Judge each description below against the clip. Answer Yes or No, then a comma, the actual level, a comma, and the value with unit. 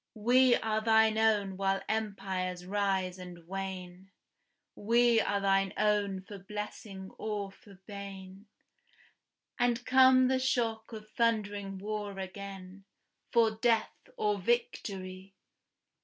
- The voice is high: Yes, high, 200 Hz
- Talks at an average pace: No, slow, 110 wpm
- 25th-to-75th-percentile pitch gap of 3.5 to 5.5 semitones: No, narrow, 2.5 semitones